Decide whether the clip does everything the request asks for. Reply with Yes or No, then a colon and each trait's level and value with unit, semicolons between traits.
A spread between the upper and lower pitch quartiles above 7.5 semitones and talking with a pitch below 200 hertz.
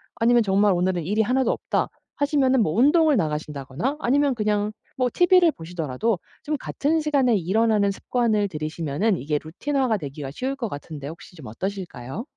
No: wide, 8.3 semitones; high, 210 Hz